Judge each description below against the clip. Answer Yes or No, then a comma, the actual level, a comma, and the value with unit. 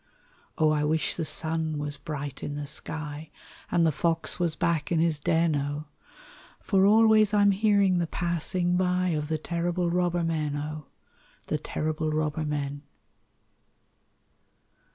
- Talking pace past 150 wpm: No, average, 145 wpm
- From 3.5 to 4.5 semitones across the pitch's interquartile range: No, average, 2.7 semitones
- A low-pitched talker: No, medium, 160 Hz